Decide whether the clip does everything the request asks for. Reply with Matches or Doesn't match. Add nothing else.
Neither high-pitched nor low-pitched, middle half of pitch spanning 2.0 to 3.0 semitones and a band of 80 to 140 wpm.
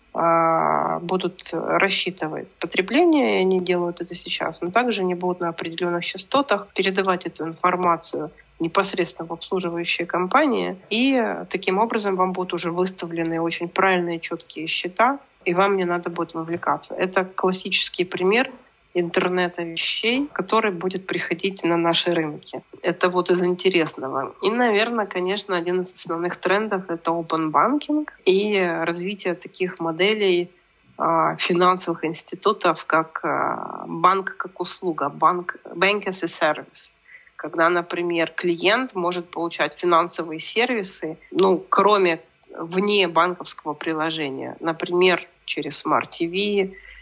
Matches